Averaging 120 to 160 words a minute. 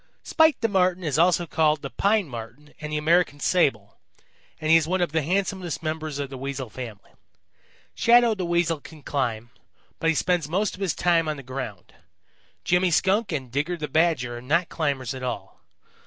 No: average, 190 wpm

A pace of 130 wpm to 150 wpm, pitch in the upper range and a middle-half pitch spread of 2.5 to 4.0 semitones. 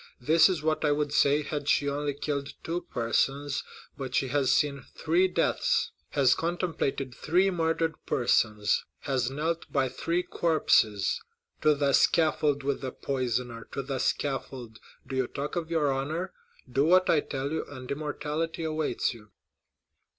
No: average, 145 wpm; medium, 145 Hz; average, 3.1 semitones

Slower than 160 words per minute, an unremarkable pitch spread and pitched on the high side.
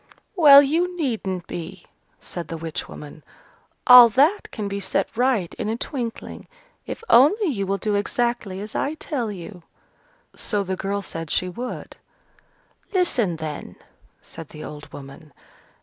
No: average, 150 wpm; wide, 6.5 semitones; high, 205 Hz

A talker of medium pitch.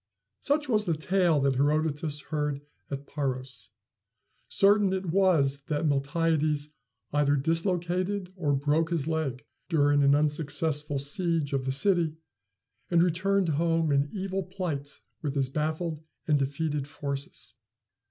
Yes: medium, 155 Hz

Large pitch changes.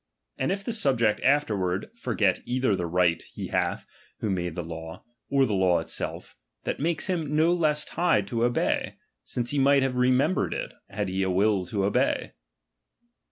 Yes: wide, 7.2 semitones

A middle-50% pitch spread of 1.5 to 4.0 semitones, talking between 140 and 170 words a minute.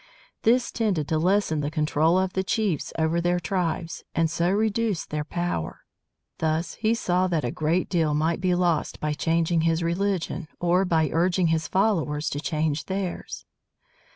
Yes: average, 2.8 semitones; average, 165 wpm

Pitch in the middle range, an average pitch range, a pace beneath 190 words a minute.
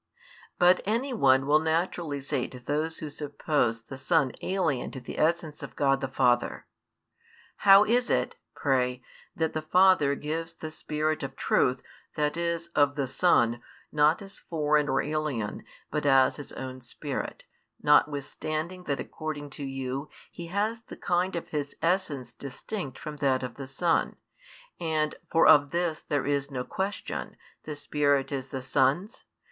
Yes: medium, 150 Hz; average, 3.7 semitones; average, 160 wpm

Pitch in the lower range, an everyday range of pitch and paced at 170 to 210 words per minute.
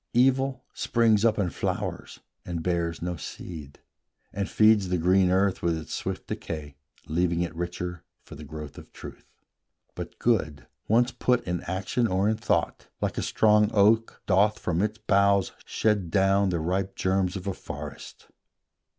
No: very low, 95 Hz; average, 3.7 semitones; average, 160 wpm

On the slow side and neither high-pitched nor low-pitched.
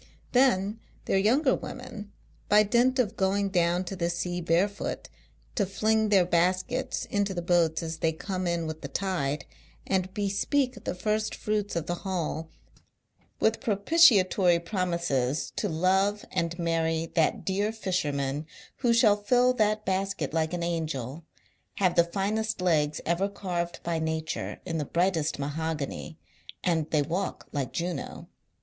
No: average, 145 wpm; medium, 180 Hz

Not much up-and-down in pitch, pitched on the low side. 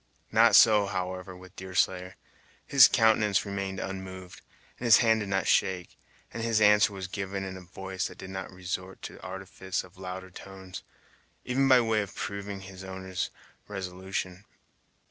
Yes: narrow, 1.7 semitones; very low, 95 Hz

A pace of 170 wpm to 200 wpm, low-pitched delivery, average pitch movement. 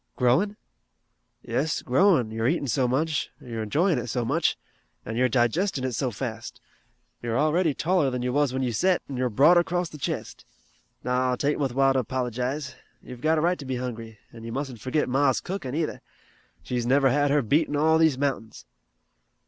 Yes: average, 195 wpm; low, 130 Hz; average, 3.7 semitones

